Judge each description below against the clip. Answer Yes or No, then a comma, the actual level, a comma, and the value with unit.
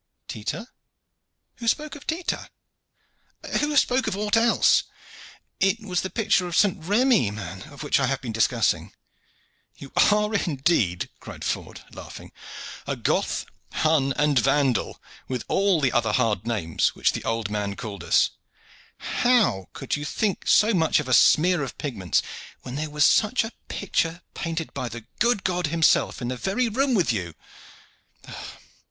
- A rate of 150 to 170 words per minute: Yes, average, 160 wpm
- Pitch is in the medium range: Yes, medium, 155 Hz